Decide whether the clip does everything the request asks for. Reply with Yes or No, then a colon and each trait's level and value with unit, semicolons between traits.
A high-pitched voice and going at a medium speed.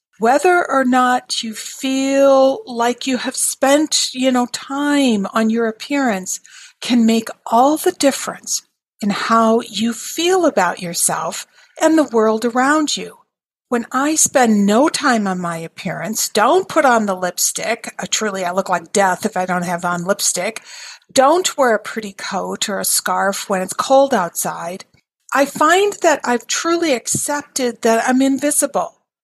Yes: high, 245 Hz; average, 160 wpm